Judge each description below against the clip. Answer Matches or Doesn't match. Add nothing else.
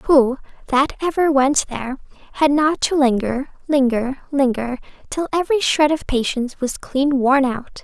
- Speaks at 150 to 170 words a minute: Matches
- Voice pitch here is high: Matches